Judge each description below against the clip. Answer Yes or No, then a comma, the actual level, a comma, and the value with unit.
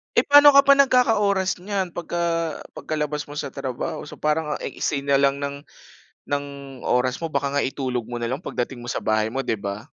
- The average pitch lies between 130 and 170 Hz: Yes, medium, 140 Hz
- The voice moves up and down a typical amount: No, wide, 6.0 semitones